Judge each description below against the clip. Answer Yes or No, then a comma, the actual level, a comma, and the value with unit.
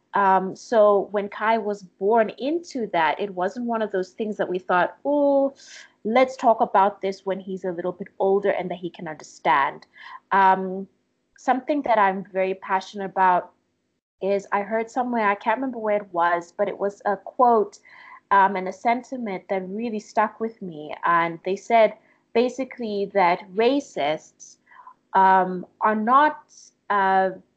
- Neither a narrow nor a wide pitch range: Yes, average, 3.5 semitones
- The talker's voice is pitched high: Yes, high, 200 Hz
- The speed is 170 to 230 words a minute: No, average, 160 wpm